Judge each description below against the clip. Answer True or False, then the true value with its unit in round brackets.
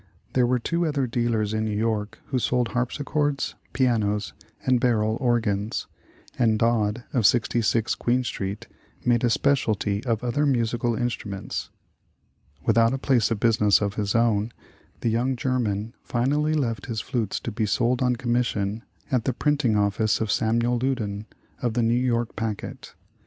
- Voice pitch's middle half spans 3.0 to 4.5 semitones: False (2.5 semitones)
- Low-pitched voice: True (115 Hz)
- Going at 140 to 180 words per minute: True (160 wpm)